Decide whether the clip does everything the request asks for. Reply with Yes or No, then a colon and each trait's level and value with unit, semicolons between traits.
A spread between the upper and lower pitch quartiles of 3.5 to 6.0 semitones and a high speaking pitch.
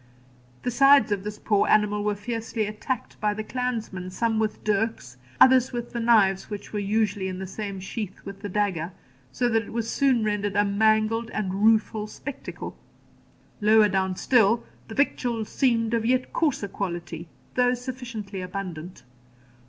No: average, 2.8 semitones; high, 215 Hz